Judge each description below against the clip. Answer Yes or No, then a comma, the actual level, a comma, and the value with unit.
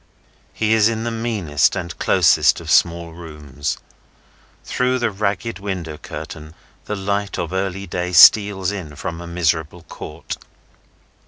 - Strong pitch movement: No, average, 3.9 semitones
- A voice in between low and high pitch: No, very low, 90 Hz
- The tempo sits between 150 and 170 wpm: No, average, 140 wpm